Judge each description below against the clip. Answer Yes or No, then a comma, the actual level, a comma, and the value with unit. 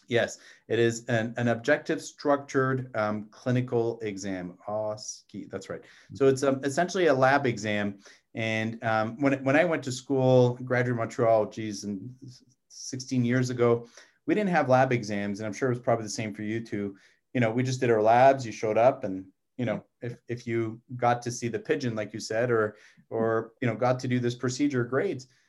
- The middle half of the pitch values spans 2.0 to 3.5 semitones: Yes, average, 2.9 semitones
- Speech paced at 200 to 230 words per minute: Yes, fast, 205 wpm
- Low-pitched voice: Yes, low, 120 Hz